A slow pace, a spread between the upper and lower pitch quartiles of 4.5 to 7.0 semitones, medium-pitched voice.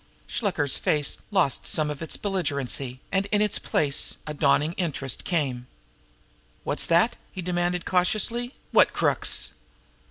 Yes: slow, 130 wpm; average, 5.1 semitones; medium, 170 Hz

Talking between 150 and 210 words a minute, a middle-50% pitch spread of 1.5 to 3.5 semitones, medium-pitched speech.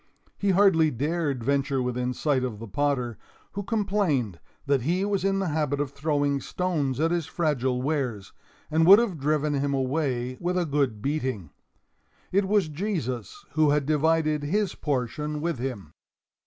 No: average, 160 wpm; average, 4.5 semitones; medium, 145 Hz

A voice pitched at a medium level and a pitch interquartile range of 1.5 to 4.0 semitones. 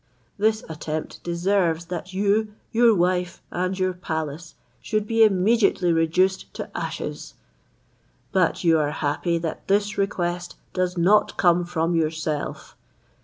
Yes: medium, 180 Hz; average, 3.2 semitones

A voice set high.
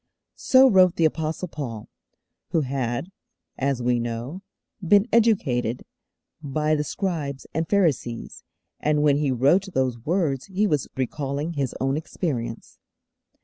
No: medium, 150 Hz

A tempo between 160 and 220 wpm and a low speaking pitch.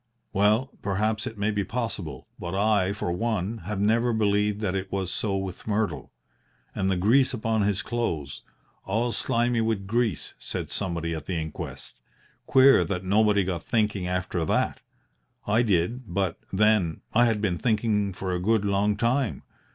Yes: average, 165 wpm; low, 105 Hz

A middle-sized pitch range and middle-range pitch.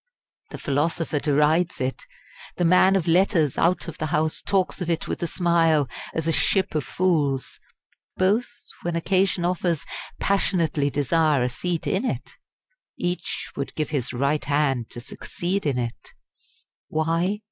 Yes: average, 3.6 semitones; medium, 165 Hz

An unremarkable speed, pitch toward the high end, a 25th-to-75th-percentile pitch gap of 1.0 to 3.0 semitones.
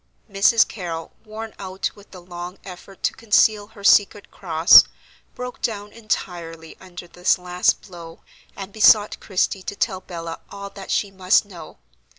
Yes: average, 155 wpm; high, 195 Hz; average, 2.7 semitones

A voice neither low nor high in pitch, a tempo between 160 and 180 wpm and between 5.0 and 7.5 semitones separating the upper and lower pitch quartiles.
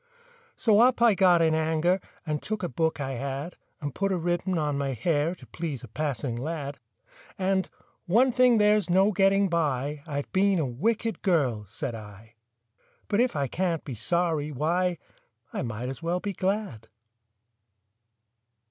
Yes: medium, 165 Hz; average, 165 wpm; wide, 5.5 semitones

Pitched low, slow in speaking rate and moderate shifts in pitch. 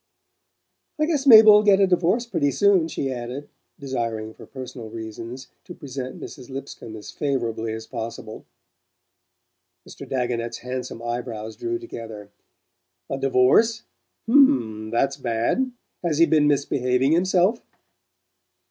No: low, 130 Hz; slow, 125 wpm; wide, 7.2 semitones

